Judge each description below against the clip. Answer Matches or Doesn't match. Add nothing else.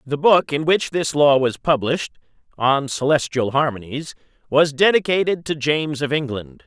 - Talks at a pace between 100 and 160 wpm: Matches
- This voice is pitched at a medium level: Matches